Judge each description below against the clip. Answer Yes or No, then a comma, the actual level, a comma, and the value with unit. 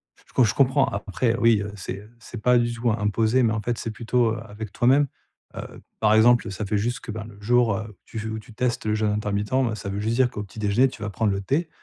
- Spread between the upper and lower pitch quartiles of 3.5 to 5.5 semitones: No, narrow, 2.5 semitones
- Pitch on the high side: No, low, 110 Hz